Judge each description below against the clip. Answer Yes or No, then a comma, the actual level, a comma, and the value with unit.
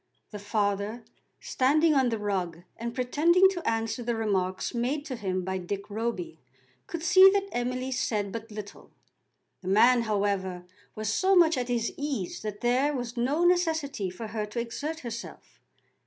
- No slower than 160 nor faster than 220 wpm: Yes, average, 165 wpm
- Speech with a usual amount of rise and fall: No, wide, 5.7 semitones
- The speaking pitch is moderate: No, high, 235 Hz